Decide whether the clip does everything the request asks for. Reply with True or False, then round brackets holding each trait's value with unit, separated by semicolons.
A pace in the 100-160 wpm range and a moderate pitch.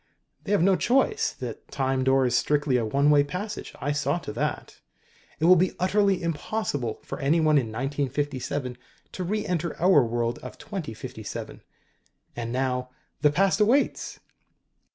True (155 wpm; 145 Hz)